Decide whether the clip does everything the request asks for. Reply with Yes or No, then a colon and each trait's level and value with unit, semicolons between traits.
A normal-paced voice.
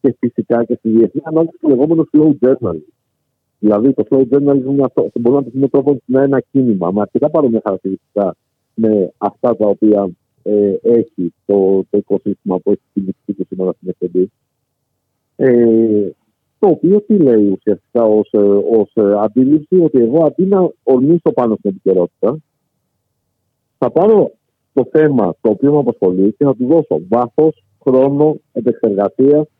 Yes: average, 150 wpm